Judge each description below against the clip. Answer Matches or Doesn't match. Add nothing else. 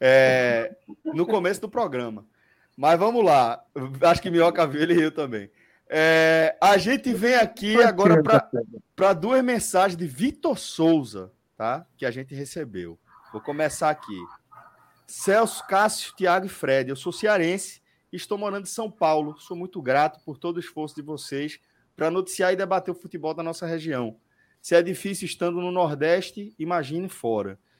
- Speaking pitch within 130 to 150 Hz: Doesn't match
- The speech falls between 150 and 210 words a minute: Matches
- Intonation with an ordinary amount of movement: Matches